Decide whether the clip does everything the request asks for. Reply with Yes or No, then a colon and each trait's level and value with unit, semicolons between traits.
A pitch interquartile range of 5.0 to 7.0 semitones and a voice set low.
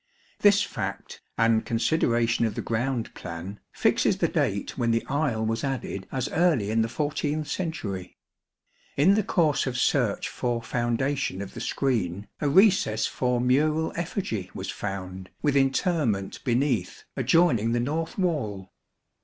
Yes: wide, 5.5 semitones; low, 125 Hz